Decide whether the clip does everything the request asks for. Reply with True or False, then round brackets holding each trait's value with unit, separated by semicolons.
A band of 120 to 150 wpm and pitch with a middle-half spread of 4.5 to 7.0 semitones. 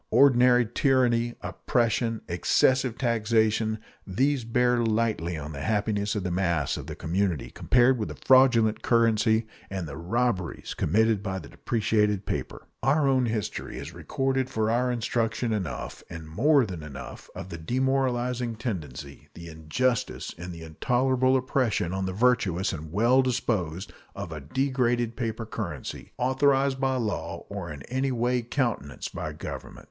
True (145 wpm; 5.1 semitones)